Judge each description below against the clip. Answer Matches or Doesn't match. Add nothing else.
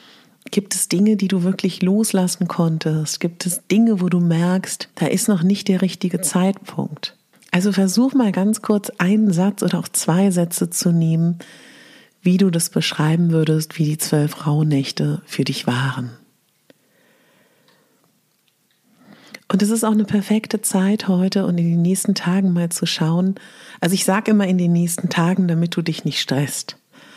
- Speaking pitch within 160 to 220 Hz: Matches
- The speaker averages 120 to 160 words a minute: Doesn't match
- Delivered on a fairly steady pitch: Doesn't match